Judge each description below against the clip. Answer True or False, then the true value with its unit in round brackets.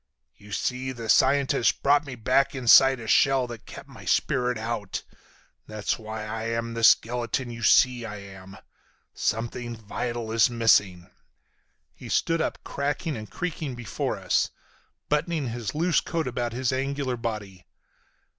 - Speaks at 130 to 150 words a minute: True (145 wpm)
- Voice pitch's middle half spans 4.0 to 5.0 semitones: False (3.2 semitones)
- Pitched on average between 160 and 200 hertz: False (120 Hz)